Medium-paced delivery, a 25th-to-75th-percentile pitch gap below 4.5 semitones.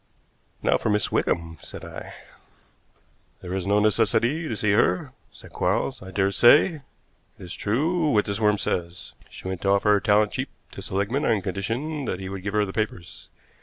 Yes: average, 190 wpm; average, 3.0 semitones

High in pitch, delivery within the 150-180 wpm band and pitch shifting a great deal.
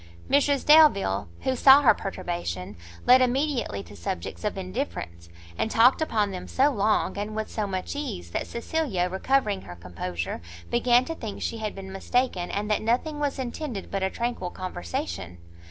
Yes: high, 215 Hz; average, 170 wpm; wide, 6.4 semitones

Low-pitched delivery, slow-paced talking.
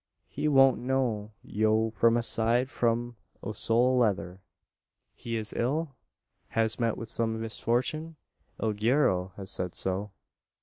Yes: low, 115 Hz; slow, 130 wpm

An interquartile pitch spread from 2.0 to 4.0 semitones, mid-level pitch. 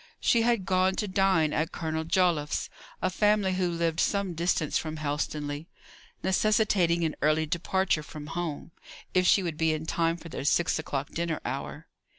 Yes: average, 3.1 semitones; medium, 170 Hz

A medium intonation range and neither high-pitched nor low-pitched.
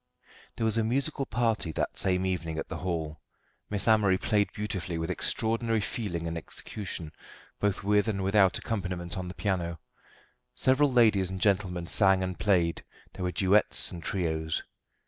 No: average, 3.5 semitones; very low, 95 Hz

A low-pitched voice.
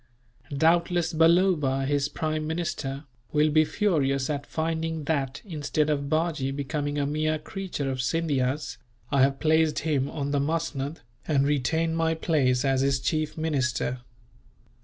No: medium, 150 Hz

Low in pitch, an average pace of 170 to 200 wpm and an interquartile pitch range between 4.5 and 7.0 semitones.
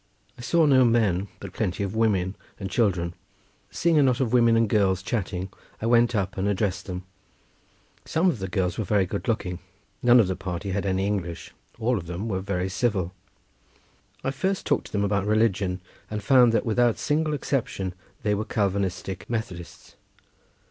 No: low, 100 Hz; average, 175 wpm; average, 3.9 semitones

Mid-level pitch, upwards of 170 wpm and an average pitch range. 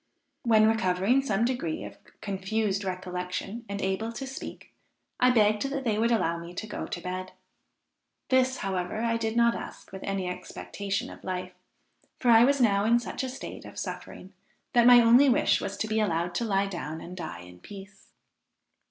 No: high, 205 Hz; average, 185 wpm; average, 4.2 semitones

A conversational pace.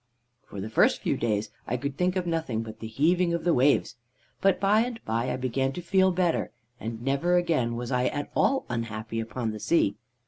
No: fast, 210 wpm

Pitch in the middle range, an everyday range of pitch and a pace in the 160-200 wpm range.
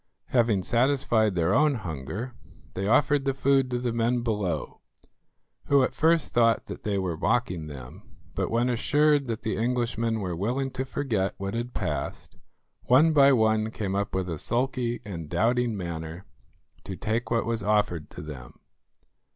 No: low, 115 Hz; average, 4.6 semitones; average, 165 wpm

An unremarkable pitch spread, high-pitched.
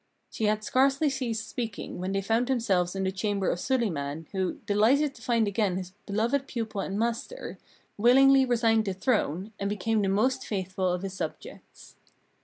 Yes: average, 4.2 semitones; high, 215 Hz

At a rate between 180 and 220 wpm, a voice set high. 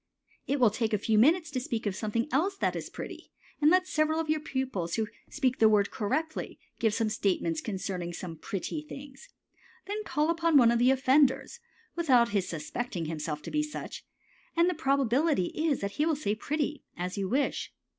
Yes: average, 190 wpm; very high, 260 Hz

